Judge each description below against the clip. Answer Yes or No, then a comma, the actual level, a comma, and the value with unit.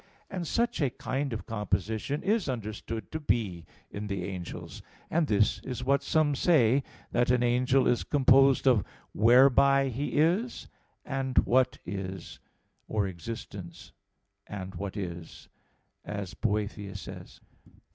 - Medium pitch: No, low, 120 Hz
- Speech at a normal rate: No, slow, 130 wpm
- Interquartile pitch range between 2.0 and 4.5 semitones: No, average, 5.2 semitones